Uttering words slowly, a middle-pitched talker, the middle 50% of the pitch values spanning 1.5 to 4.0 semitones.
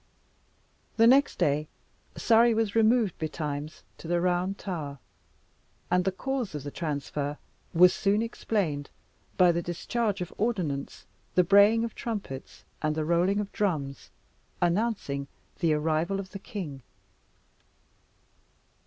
No: slow, 125 wpm; medium, 180 Hz; wide, 5.4 semitones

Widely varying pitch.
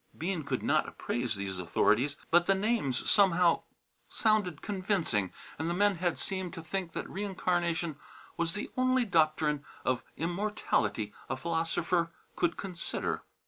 No: average, 3.9 semitones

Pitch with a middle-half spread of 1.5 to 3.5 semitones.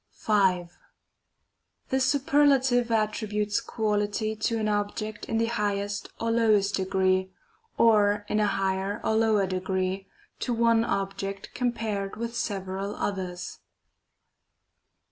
Yes: narrow, 2.6 semitones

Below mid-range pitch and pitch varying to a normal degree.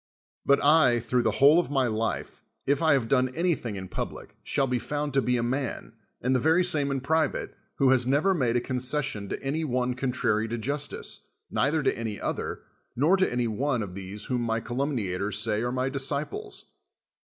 Yes: low, 130 Hz; average, 3.6 semitones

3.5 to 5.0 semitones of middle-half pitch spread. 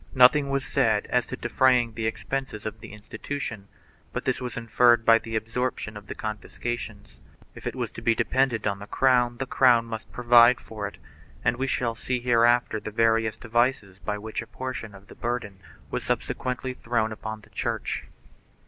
No: narrow, 2.4 semitones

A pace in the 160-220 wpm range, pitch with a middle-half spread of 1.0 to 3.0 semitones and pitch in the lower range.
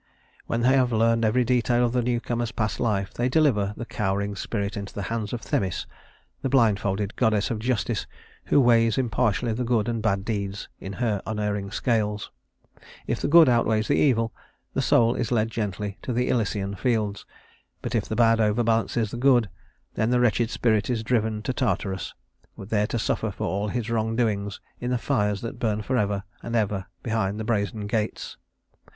Yes: average, 180 wpm; narrow, 2.6 semitones; low, 110 Hz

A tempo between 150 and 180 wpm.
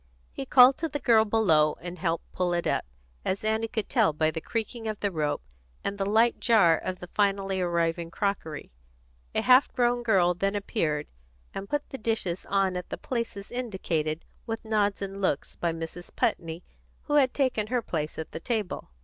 No: average, 190 wpm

